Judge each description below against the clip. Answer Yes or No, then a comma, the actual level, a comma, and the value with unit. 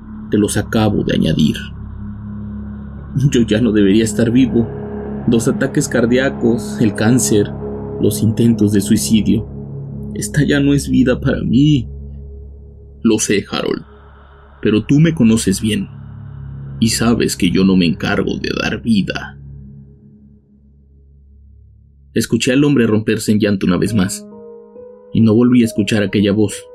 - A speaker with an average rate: Yes, average, 135 wpm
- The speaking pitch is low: Yes, low, 105 Hz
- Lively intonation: Yes, wide, 8.8 semitones